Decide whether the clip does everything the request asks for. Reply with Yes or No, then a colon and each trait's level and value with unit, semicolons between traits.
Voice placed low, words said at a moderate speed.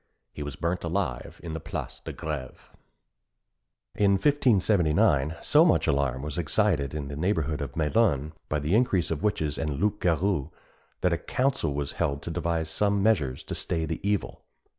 Yes: very low, 80 Hz; average, 170 wpm